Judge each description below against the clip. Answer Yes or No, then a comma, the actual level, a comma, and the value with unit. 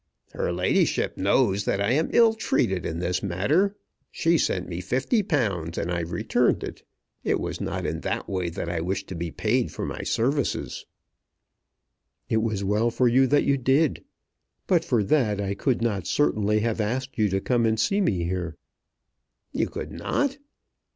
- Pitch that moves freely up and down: Yes, wide, 6.1 semitones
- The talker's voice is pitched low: Yes, low, 110 Hz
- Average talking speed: Yes, average, 175 wpm